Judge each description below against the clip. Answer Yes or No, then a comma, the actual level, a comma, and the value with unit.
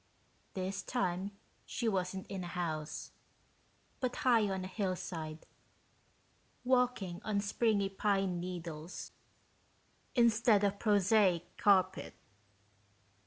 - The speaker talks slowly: Yes, slow, 95 wpm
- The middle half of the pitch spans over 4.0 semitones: No, average, 3.0 semitones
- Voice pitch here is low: No, high, 195 Hz